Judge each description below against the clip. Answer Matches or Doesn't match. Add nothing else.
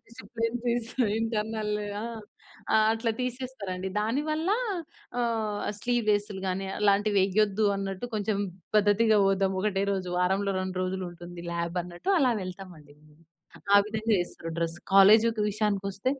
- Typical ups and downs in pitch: Matches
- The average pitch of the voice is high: Matches